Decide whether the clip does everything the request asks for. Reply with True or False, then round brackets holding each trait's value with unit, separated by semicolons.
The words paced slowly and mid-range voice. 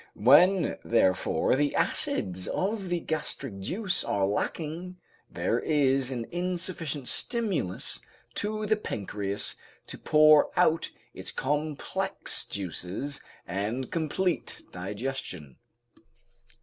True (95 wpm; 145 Hz)